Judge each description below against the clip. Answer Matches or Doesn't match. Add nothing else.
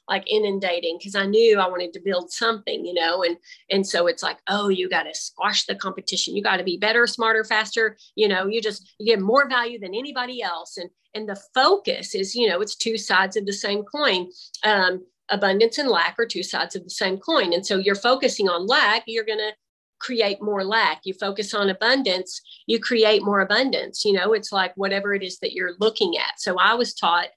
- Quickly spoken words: Matches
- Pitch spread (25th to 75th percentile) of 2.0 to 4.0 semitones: Matches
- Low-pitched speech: Doesn't match